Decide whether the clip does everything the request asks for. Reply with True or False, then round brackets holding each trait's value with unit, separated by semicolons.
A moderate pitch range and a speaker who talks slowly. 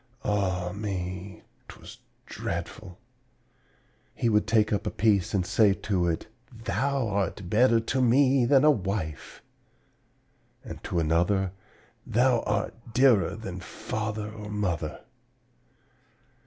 True (3.6 semitones; 115 wpm)